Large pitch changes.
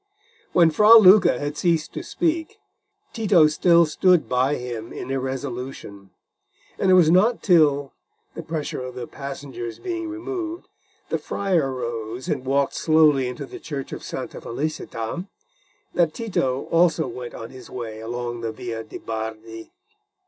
Yes: wide, 6.3 semitones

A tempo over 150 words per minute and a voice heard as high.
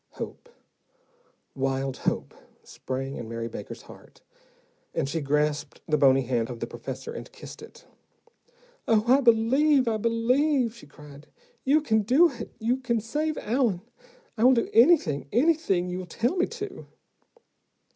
No: average, 145 wpm; high, 225 Hz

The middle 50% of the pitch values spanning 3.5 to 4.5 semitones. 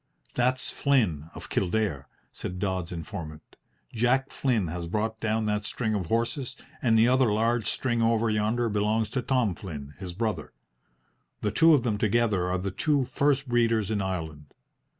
Yes: average, 4.2 semitones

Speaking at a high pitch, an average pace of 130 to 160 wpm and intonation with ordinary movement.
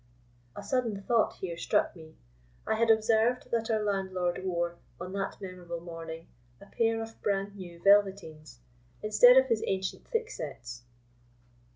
Yes: high, 195 Hz; average, 145 wpm; average, 4.5 semitones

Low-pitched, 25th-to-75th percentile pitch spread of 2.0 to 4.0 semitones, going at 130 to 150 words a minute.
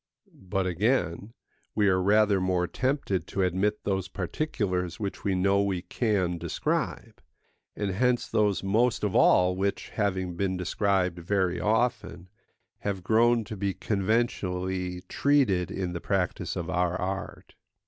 Yes: very low, 95 Hz; narrow, 2.5 semitones; average, 140 wpm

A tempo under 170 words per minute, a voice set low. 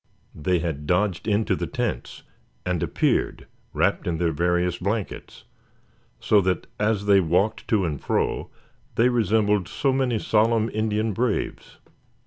Yes: slow, 135 wpm; low, 100 Hz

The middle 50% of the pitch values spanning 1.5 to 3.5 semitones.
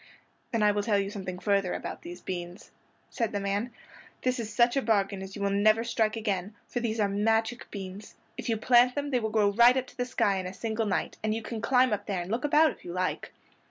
Yes: average, 3.1 semitones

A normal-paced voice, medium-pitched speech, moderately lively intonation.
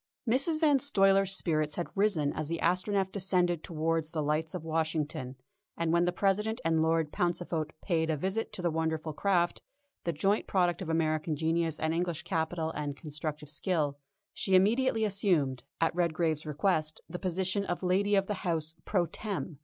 Yes: average, 170 wpm; medium, 170 Hz; average, 3.5 semitones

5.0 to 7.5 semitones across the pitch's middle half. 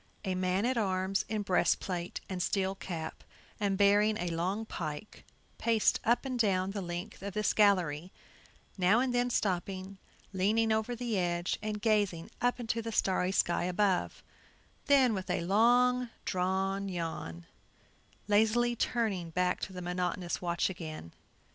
No: average, 3.4 semitones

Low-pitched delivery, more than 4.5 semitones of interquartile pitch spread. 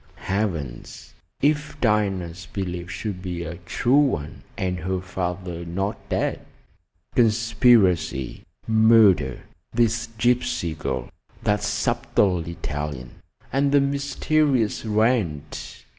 Yes: very low, 95 Hz; average, 5.2 semitones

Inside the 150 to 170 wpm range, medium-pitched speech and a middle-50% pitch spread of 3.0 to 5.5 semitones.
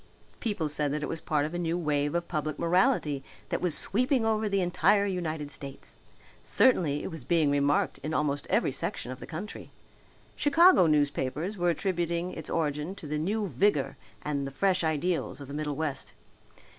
No: average, 180 wpm; medium, 160 Hz; average, 3.9 semitones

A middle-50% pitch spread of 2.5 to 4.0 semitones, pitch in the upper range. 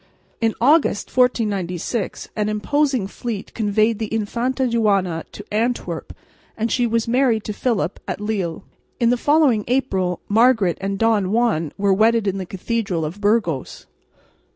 Yes: average, 3.2 semitones; high, 215 Hz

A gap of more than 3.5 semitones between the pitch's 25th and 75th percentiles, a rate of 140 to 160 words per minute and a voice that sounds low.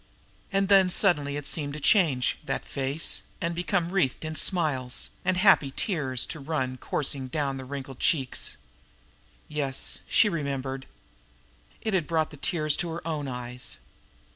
No: average, 4.3 semitones; average, 150 wpm; medium, 150 Hz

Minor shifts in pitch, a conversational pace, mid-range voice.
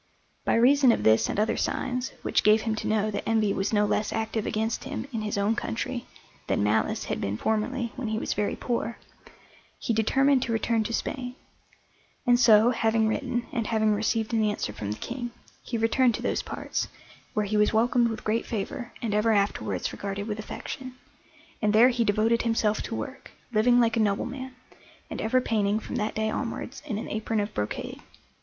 No: narrow, 2.2 semitones; average, 195 wpm; high, 220 Hz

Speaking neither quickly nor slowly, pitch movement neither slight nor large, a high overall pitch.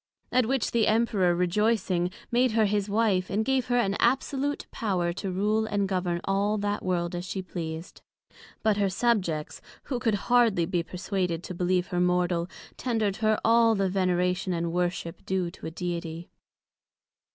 Yes: average, 165 wpm; average, 3.7 semitones; high, 195 Hz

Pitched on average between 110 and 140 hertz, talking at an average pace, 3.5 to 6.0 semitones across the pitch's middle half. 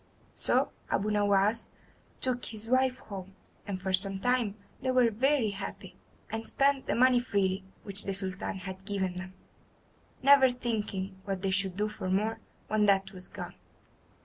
No: high, 205 Hz; average, 160 wpm; average, 3.9 semitones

